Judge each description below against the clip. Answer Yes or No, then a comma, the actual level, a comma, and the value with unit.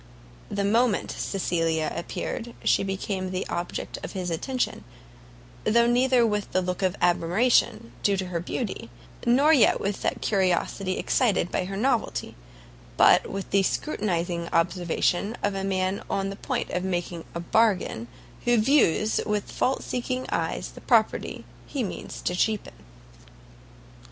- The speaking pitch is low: No, high, 195 Hz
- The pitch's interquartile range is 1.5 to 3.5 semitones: No, average, 4.3 semitones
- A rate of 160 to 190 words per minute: No, average, 145 wpm